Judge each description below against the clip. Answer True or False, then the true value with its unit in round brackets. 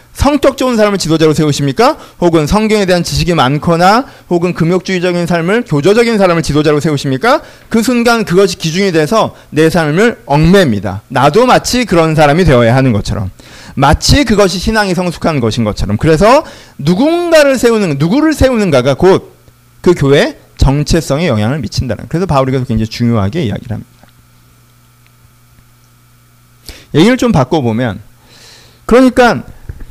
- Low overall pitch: False (160 Hz)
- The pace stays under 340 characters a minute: False (350 characters per minute)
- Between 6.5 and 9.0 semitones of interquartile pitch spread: True (8.4 semitones)